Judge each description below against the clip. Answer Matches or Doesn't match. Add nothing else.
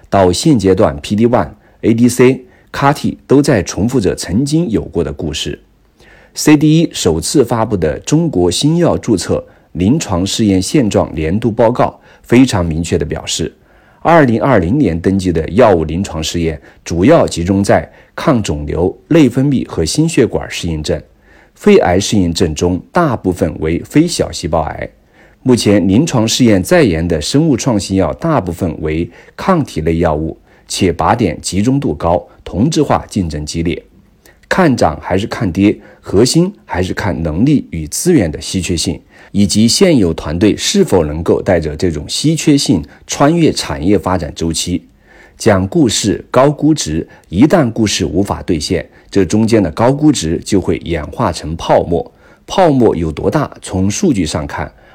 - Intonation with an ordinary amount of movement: Doesn't match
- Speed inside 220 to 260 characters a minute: Matches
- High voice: Doesn't match